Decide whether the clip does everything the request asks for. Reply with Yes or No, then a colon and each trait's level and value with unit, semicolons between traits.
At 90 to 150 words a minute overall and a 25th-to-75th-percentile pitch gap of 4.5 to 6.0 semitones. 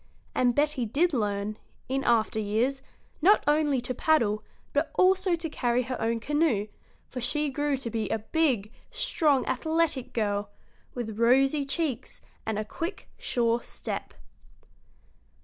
Yes: average, 140 wpm; average, 5.0 semitones